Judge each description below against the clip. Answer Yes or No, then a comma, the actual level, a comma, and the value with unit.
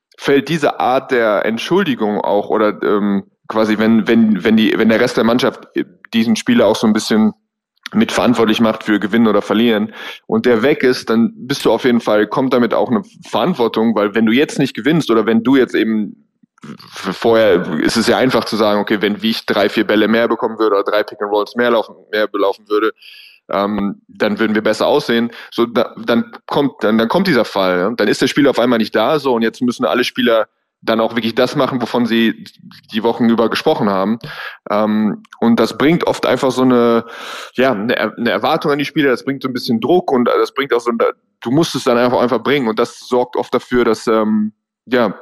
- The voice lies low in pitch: Yes, low, 115 Hz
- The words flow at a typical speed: No, fast, 220 wpm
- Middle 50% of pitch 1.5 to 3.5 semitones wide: No, average, 4.2 semitones